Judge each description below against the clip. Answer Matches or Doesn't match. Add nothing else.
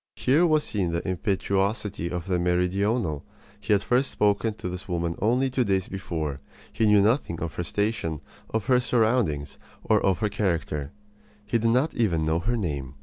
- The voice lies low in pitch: Matches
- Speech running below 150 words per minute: Doesn't match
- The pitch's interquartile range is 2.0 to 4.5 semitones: Doesn't match